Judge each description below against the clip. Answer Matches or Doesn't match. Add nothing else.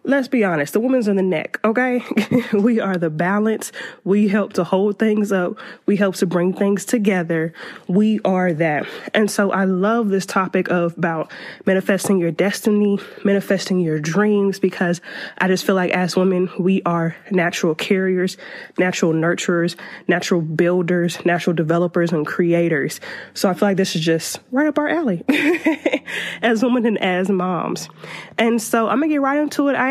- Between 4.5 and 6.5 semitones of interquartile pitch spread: Doesn't match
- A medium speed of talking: Matches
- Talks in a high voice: Matches